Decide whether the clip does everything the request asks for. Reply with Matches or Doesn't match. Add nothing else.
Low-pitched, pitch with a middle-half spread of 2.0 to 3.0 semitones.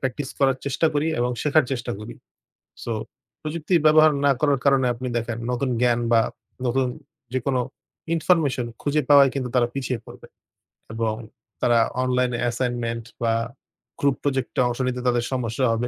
Matches